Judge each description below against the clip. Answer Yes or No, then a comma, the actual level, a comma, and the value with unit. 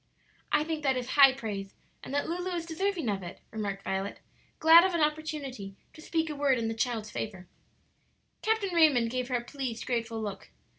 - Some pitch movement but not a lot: No, wide, 6.2 semitones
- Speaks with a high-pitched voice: Yes, very high, 265 Hz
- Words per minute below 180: No, average, 195 wpm